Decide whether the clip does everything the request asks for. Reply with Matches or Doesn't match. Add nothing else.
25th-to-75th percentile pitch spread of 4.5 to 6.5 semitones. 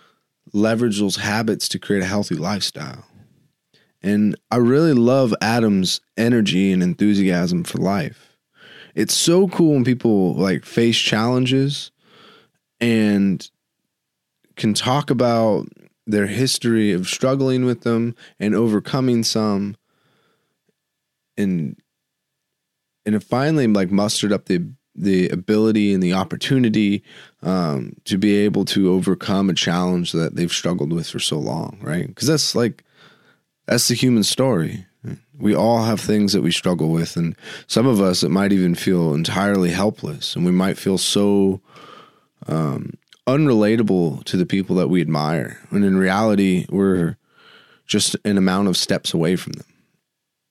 Doesn't match